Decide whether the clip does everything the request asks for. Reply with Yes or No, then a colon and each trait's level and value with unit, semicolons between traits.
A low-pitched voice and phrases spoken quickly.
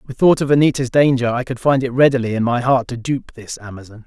Yes: low, 125 Hz; fast, 250 wpm